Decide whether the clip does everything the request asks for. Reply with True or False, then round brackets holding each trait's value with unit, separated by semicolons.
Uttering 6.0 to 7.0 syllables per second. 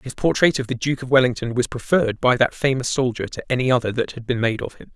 True (6.4 syllables/s)